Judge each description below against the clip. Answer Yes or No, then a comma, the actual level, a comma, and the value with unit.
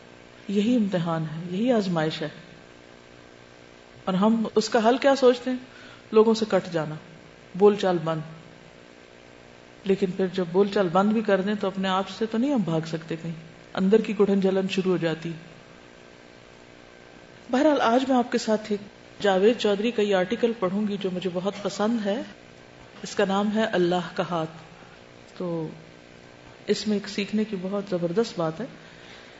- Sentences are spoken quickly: No, average, 165 wpm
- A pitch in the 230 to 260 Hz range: No, medium, 185 Hz